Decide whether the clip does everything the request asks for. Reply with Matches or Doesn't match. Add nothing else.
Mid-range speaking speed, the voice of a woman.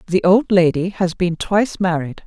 Matches